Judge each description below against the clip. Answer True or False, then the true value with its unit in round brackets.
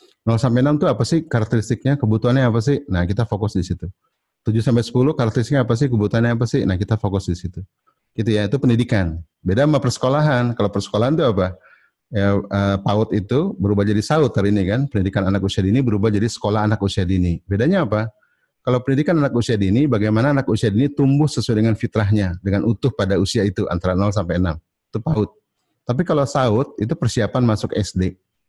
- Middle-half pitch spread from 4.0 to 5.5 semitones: True (4.4 semitones)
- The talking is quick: True (195 wpm)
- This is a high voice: False (110 Hz)